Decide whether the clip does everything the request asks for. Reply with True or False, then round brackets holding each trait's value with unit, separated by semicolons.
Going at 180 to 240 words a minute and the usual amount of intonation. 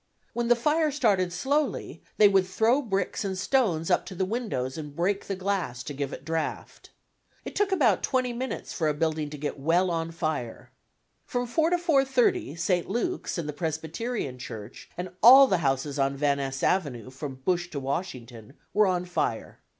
False (185 wpm; 8.2 semitones)